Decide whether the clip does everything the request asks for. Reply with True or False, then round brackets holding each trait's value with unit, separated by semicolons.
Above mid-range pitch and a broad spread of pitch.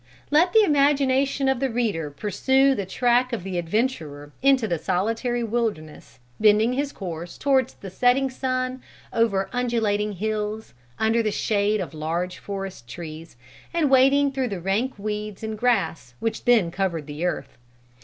True (220 Hz; 5.8 semitones)